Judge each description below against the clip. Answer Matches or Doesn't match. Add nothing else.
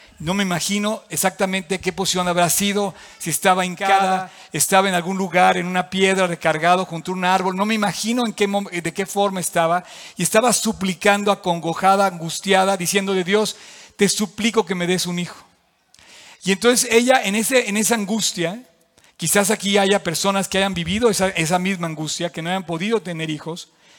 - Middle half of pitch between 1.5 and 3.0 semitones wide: Matches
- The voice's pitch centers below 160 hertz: Doesn't match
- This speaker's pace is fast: Doesn't match